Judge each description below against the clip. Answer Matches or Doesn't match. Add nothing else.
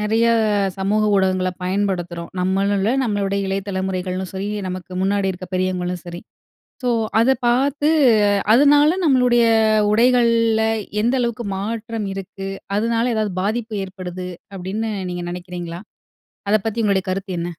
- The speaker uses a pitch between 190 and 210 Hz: Matches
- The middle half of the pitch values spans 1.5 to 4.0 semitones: Matches